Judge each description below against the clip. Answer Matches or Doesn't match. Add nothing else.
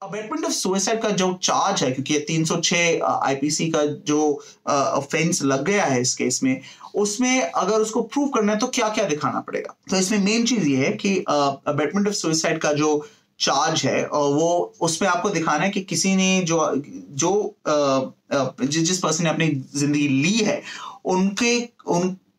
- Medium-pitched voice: Matches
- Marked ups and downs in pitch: Matches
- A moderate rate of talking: Matches